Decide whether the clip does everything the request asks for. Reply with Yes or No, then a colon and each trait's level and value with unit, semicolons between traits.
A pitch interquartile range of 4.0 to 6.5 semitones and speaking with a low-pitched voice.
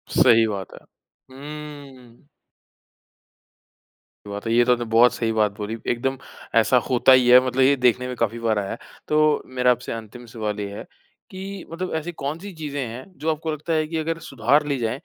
Yes: average, 4.7 semitones; low, 125 Hz